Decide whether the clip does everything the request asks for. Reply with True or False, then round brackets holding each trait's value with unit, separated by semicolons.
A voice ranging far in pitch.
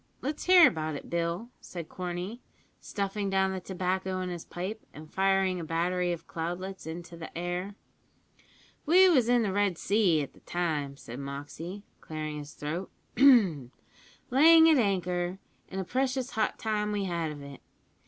False (4.0 semitones)